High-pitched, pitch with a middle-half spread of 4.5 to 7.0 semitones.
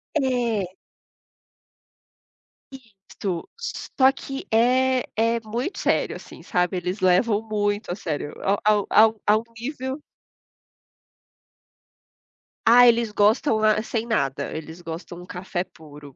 Yes: high, 215 Hz; average, 4.9 semitones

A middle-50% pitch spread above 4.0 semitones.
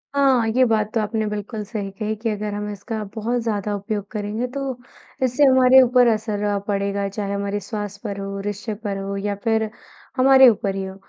No: narrow, 2.6 semitones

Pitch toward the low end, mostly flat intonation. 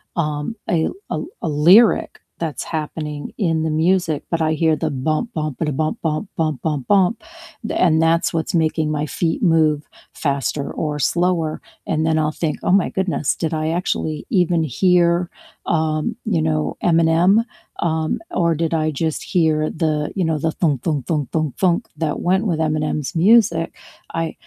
No: medium, 160 Hz; narrow, 2.0 semitones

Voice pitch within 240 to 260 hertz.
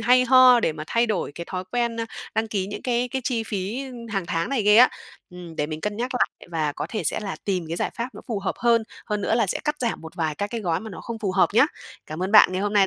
No: high, 210 Hz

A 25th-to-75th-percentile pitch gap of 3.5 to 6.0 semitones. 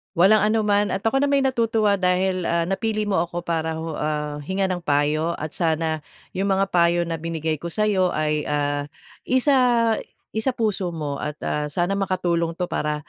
Yes: average, 4.5 semitones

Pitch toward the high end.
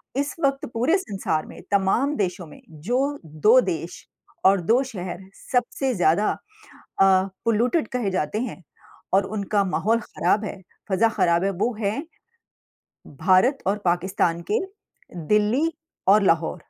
Yes: high, 205 Hz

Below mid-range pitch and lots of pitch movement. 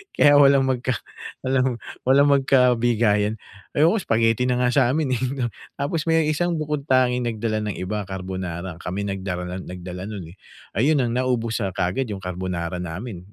Yes: low, 115 Hz; wide, 5.9 semitones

